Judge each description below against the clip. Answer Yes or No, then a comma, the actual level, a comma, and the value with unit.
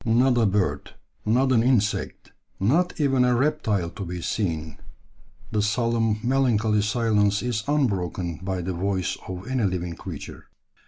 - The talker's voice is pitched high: No, low, 105 Hz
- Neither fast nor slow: Yes, average, 145 wpm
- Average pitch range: Yes, average, 4.7 semitones